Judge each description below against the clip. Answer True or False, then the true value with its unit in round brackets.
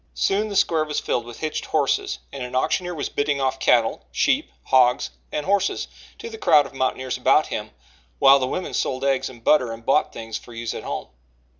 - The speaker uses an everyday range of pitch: True (3.8 semitones)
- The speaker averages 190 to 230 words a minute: True (205 wpm)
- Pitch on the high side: False (135 Hz)